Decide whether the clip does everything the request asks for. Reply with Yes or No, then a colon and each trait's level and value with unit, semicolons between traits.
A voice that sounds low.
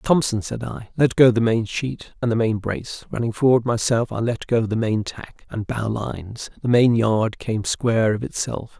Yes: low, 115 Hz